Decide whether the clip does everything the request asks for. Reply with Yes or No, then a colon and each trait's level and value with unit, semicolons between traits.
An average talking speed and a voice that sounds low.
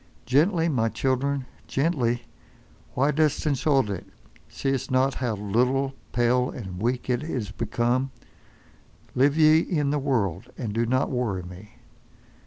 No: slow, 125 wpm; low, 130 Hz